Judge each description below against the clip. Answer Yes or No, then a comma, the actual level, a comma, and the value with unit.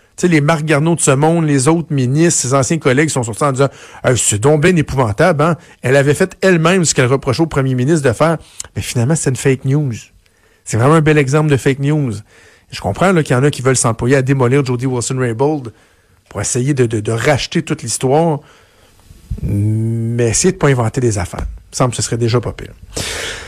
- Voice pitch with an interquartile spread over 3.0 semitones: Yes, average, 4.7 semitones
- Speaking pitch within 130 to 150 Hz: Yes, low, 135 Hz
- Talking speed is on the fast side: Yes, fast, 225 wpm